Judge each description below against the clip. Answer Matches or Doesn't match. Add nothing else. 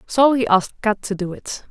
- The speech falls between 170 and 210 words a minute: Doesn't match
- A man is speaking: Doesn't match